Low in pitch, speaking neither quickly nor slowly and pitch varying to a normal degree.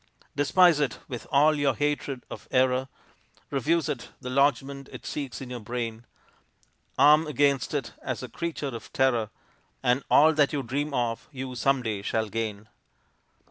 Yes: low, 130 Hz; average, 165 wpm; average, 3.2 semitones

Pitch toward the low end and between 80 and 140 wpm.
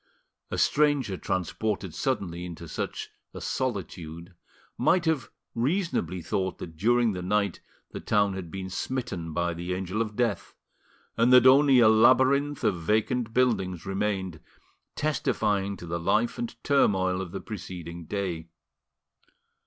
Yes: low, 100 Hz; slow, 135 wpm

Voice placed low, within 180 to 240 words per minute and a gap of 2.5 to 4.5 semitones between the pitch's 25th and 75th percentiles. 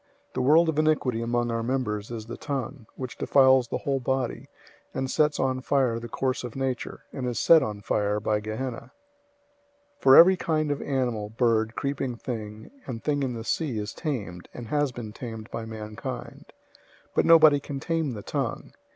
Yes: low, 125 Hz; average, 190 wpm; average, 3.7 semitones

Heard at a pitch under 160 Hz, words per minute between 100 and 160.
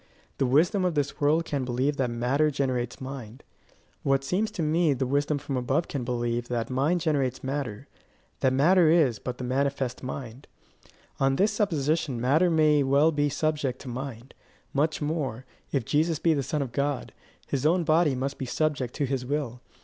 No: medium, 140 Hz; average, 180 wpm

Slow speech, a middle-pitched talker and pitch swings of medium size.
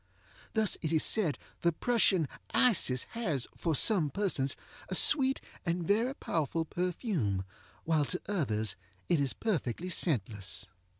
No: slow, 130 wpm; medium, 165 Hz; wide, 6.9 semitones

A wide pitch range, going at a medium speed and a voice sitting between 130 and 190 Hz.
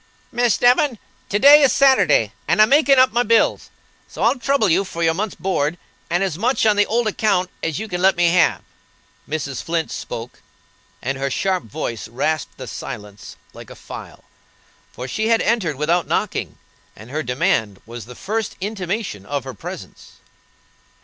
Yes: wide, 7.8 semitones; average, 175 wpm; medium, 185 Hz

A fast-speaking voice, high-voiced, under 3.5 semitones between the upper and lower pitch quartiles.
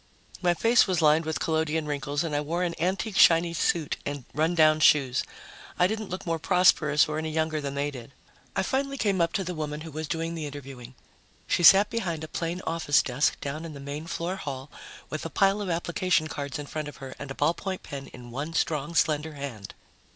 No: fast, 215 wpm; medium, 155 Hz; average, 2.9 semitones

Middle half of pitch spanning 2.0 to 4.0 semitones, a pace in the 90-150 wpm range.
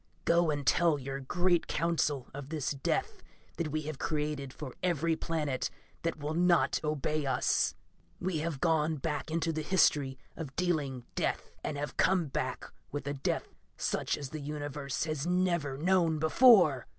No: average, 2.9 semitones; average, 165 wpm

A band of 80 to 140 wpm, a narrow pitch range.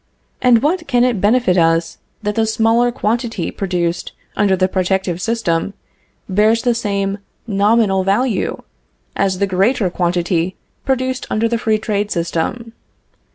No: slow, 135 wpm; average, 3.9 semitones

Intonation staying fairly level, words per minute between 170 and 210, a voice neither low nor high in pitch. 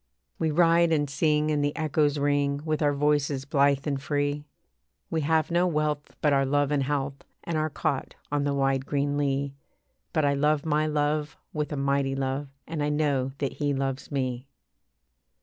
Yes: narrow, 1.5 semitones; average, 185 wpm; medium, 145 Hz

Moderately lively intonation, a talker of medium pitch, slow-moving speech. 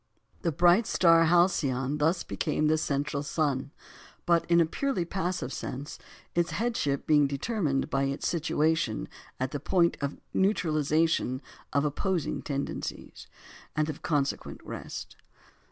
Yes: average, 3.5 semitones; medium, 155 Hz; slow, 130 wpm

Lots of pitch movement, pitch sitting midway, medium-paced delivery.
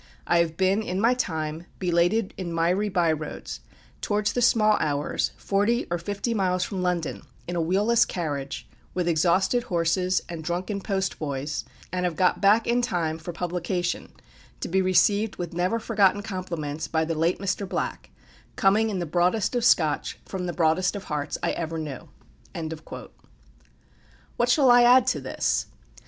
No: average, 3.6 semitones; medium, 180 Hz; average, 165 wpm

